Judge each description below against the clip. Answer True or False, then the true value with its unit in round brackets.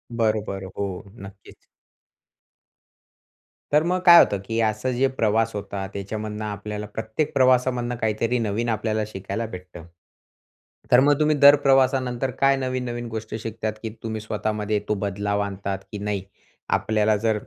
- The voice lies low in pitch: True (110 Hz)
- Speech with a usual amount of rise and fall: True (3.2 semitones)